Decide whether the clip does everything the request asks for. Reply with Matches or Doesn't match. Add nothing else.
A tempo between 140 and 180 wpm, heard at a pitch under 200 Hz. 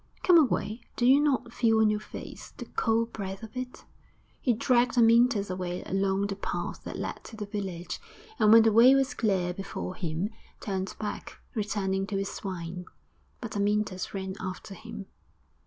Doesn't match